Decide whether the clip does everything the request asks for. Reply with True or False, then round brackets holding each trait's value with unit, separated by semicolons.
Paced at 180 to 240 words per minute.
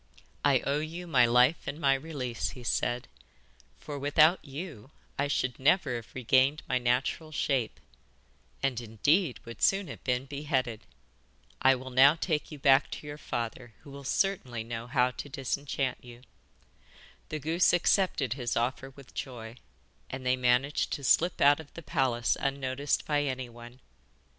False (155 wpm)